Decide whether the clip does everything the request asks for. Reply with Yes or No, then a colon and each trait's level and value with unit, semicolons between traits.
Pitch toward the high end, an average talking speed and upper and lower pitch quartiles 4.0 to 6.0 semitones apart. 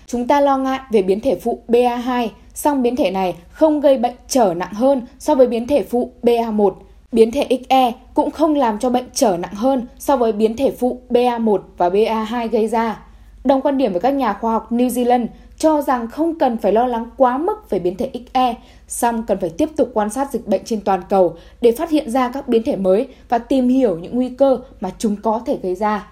No: high, 245 Hz; average, 230 wpm; average, 3.3 semitones